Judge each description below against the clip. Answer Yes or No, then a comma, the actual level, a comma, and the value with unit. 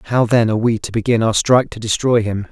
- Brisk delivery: Yes, fast, 265 wpm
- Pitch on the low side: Yes, low, 115 Hz